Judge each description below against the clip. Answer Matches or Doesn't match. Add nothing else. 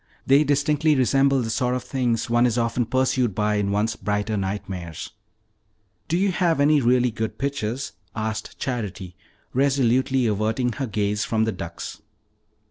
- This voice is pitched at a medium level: Doesn't match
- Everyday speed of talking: Matches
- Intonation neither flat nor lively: Matches